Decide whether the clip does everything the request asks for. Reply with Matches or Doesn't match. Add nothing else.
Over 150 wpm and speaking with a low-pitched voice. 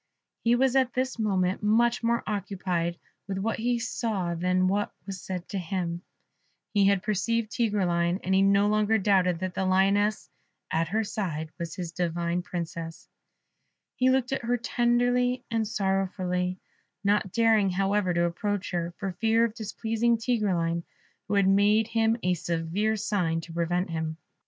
Doesn't match